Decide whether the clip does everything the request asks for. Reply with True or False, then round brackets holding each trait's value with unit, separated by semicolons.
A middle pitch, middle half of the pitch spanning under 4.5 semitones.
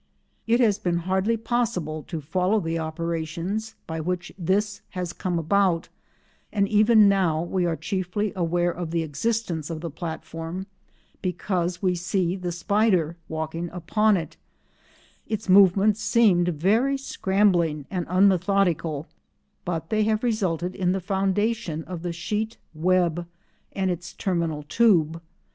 True (180 Hz; 3.5 semitones)